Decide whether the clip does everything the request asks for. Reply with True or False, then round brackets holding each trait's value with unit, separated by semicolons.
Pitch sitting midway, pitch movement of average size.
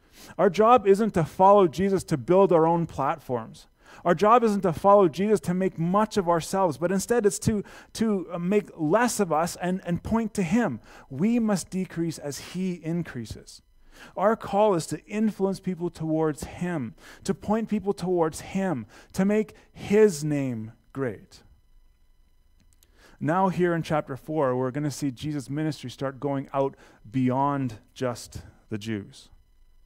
False (170 Hz; 6.4 semitones)